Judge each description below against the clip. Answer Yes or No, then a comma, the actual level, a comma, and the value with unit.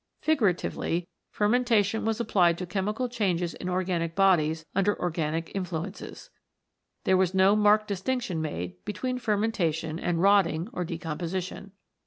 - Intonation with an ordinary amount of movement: Yes, average, 3.8 semitones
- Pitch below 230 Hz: Yes, medium, 185 Hz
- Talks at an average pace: No, slow, 125 wpm